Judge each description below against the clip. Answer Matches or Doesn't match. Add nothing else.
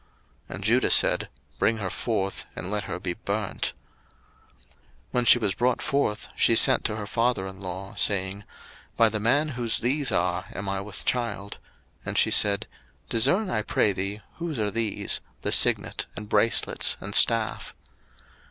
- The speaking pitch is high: Doesn't match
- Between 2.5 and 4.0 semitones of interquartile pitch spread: Matches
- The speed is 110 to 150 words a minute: Doesn't match